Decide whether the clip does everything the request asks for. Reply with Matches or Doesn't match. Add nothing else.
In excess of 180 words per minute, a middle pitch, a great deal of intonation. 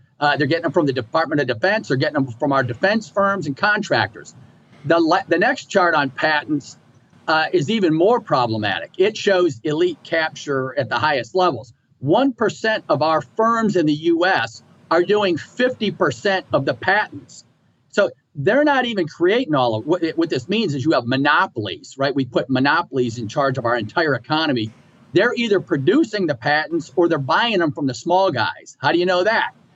Matches